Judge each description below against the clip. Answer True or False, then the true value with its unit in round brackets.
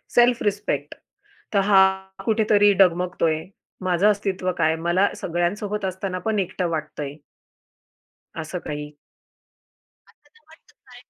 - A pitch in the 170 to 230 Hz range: True (190 Hz)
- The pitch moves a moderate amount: True (3.2 semitones)